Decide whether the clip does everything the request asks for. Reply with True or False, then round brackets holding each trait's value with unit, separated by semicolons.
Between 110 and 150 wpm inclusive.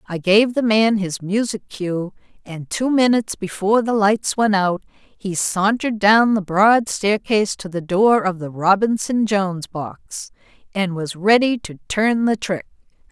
False (165 wpm)